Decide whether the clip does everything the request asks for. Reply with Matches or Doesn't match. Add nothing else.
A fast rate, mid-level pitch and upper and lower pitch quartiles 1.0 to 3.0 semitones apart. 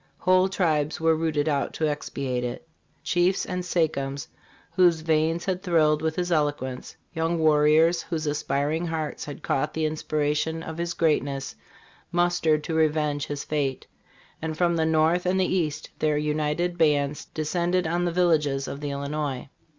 Doesn't match